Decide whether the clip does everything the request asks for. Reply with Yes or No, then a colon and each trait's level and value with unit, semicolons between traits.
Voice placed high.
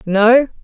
Yes: high, 230 Hz